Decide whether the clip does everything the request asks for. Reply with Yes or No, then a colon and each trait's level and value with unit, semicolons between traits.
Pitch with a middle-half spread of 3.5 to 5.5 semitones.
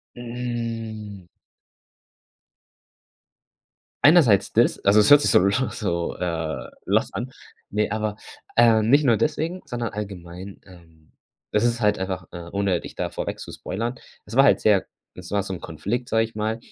Yes: average, 4.0 semitones